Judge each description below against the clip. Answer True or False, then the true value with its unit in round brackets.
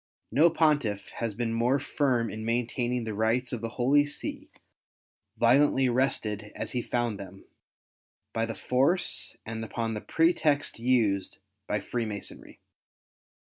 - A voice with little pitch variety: False (3.2 semitones)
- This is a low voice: True (120 Hz)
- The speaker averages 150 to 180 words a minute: False (135 wpm)